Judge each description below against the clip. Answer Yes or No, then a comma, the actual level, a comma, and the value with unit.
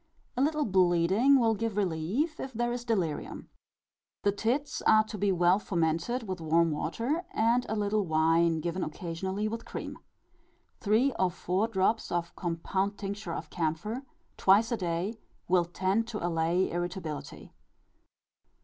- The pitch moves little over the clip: No, average, 4.9 semitones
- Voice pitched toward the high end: Yes, high, 195 Hz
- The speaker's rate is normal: Yes, average, 145 wpm